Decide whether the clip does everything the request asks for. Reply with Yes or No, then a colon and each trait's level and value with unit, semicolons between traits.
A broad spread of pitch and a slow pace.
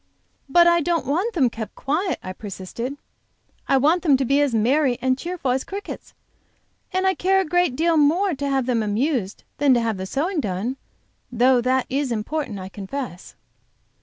No: wide, 5.9 semitones; average, 185 wpm